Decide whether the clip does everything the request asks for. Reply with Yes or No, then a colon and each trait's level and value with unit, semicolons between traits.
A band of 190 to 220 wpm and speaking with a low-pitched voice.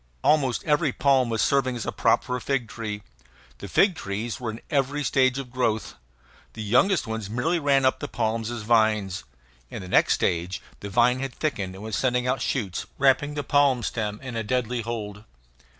Yes: average, 200 wpm; low, 120 Hz